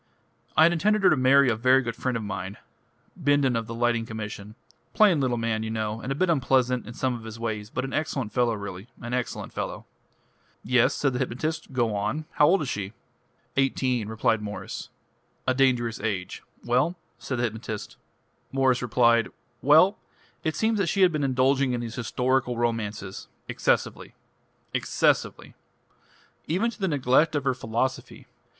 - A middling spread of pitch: Yes, average, 3.5 semitones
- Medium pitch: No, low, 125 Hz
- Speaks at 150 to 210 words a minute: Yes, average, 155 wpm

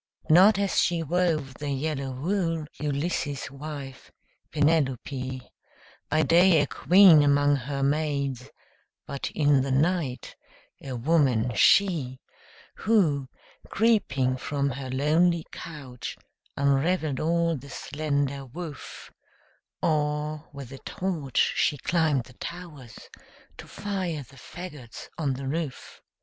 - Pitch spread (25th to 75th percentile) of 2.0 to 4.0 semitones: Yes, average, 3.6 semitones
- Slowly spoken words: Yes, slow, 115 wpm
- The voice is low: No, medium, 145 Hz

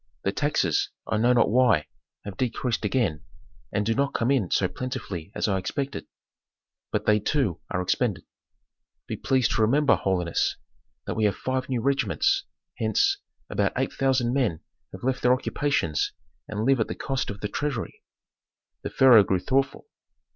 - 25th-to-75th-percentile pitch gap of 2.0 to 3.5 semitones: No, average, 4.9 semitones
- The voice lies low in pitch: Yes, low, 120 Hz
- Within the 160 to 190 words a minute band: Yes, average, 165 wpm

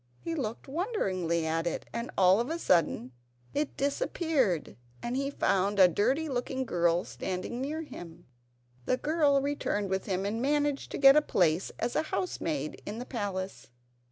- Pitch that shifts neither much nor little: No, wide, 7.6 semitones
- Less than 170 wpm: Yes, average, 160 wpm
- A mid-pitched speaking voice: No, high, 235 Hz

